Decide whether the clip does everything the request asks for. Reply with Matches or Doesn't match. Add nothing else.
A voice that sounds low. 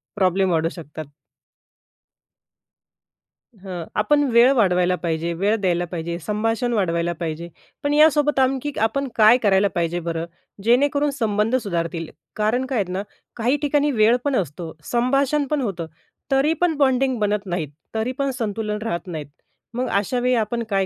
Doesn't match